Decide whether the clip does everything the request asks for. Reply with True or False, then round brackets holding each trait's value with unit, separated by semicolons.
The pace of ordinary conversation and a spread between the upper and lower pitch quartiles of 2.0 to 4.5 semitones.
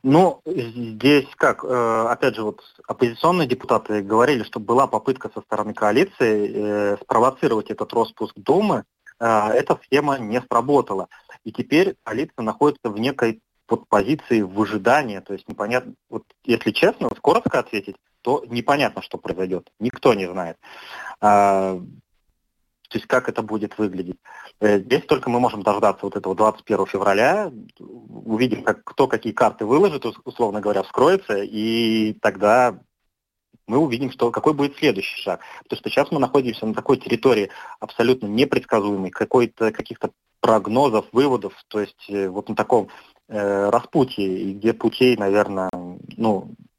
True (130 wpm; 3.5 semitones)